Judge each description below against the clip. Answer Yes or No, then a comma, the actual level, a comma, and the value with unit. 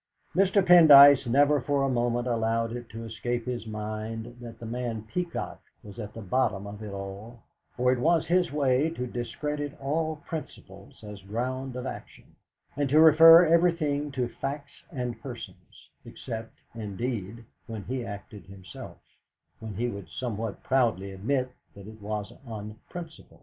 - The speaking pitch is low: Yes, low, 120 Hz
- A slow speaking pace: No, average, 155 wpm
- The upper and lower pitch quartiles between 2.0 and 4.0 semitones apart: No, average, 4.7 semitones